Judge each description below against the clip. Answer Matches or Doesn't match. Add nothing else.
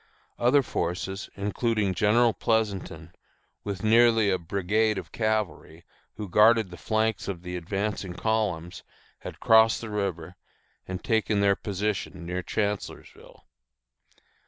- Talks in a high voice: Doesn't match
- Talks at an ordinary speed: Doesn't match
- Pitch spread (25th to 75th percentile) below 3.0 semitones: Doesn't match